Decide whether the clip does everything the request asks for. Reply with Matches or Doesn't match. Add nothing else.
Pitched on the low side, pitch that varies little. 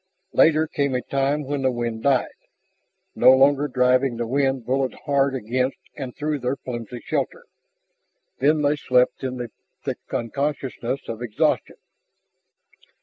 Matches